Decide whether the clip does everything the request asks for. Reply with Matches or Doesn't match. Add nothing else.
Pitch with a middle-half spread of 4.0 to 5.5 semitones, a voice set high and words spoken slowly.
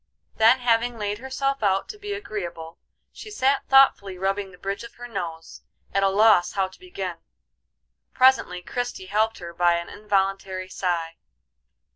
Doesn't match